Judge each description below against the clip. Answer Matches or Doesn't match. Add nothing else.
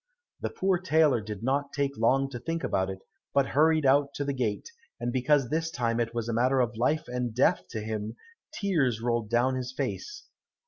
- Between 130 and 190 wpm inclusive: Doesn't match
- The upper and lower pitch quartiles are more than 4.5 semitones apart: Doesn't match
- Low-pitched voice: Matches